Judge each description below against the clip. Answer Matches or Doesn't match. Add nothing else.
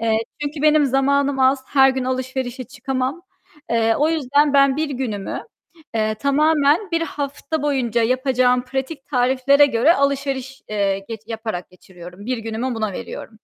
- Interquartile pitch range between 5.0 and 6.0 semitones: Doesn't match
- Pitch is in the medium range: Doesn't match